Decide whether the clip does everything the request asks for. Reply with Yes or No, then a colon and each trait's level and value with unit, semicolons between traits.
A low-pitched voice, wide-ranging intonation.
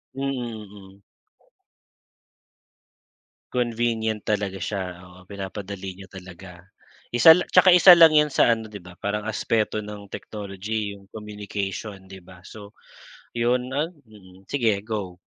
No: low, 105 Hz; average, 3.3 semitones